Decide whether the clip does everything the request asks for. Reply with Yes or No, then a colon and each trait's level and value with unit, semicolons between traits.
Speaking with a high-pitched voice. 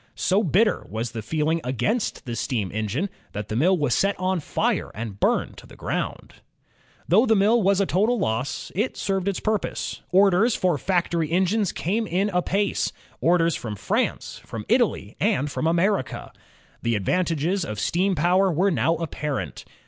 No: medium, 175 Hz